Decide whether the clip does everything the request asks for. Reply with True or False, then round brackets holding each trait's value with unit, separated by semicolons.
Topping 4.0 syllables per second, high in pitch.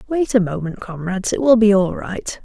True (5.3 syllables/s; 210 Hz)